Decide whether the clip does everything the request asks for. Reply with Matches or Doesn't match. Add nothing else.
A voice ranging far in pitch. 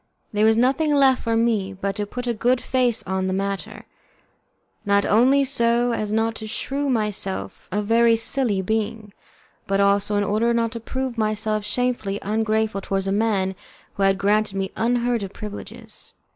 Doesn't match